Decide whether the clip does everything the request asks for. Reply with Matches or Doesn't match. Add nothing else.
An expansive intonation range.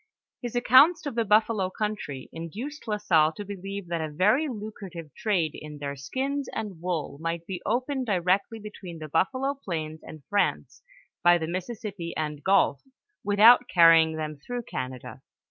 Matches